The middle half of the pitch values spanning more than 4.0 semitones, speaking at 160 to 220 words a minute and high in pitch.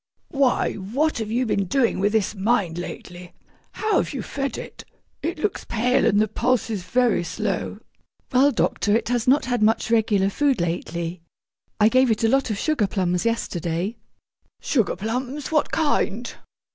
Yes: average, 4.7 semitones; average, 170 wpm; high, 225 Hz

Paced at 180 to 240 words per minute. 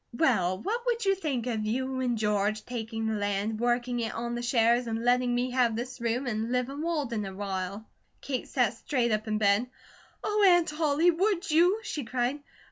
Yes: average, 195 wpm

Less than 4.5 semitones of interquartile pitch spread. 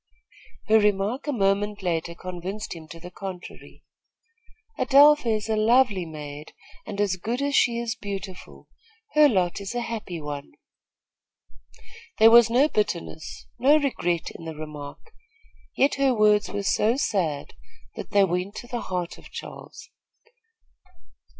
No: average, 5.1 semitones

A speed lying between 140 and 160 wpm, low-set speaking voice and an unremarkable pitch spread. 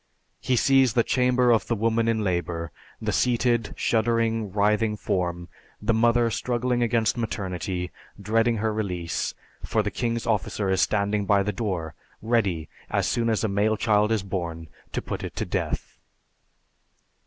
Yes: average, 155 wpm; low, 110 Hz; average, 3.1 semitones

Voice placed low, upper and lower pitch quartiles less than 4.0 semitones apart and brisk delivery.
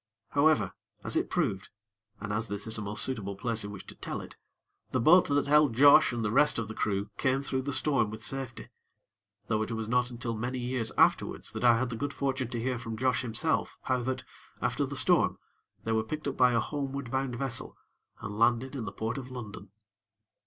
Yes: low, 120 Hz; average, 3.2 semitones; fast, 215 wpm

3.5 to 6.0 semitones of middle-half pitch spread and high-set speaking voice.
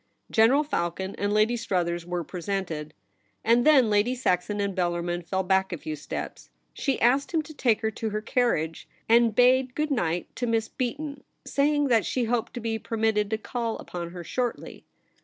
Yes: wide, 5.4 semitones; high, 220 Hz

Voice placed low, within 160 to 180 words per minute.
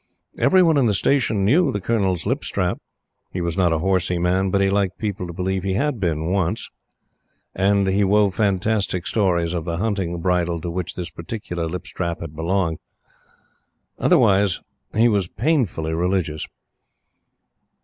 Yes: very low, 95 Hz; average, 165 wpm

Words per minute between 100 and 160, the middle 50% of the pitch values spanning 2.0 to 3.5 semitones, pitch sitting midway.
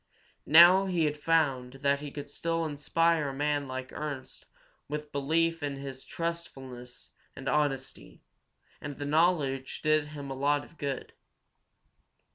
Yes: average, 140 wpm; average, 2.9 semitones; medium, 145 Hz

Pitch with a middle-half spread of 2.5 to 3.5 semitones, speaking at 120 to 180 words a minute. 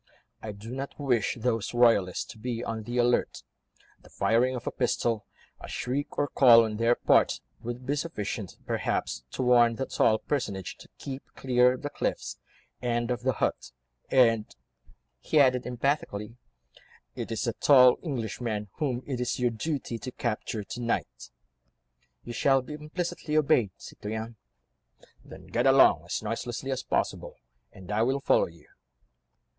Yes: average, 2.8 semitones; average, 155 wpm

